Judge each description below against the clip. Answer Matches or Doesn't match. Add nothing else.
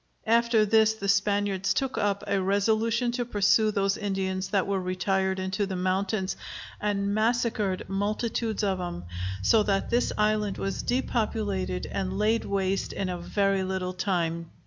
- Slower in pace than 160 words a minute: Matches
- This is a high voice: Matches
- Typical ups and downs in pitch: Doesn't match